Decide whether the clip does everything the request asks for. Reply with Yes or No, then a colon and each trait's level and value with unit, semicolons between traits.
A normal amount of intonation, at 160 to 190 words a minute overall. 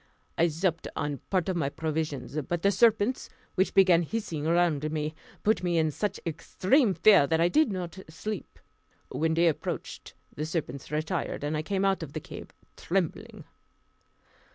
Yes: average, 3.7 semitones; average, 165 wpm